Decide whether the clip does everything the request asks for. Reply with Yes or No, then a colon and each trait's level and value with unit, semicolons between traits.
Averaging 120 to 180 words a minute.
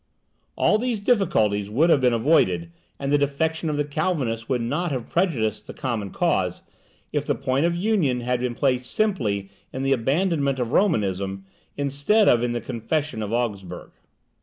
Yes: average, 170 wpm